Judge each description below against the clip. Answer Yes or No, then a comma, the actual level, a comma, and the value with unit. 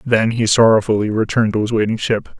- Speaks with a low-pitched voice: Yes, low, 110 Hz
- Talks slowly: No, average, 200 wpm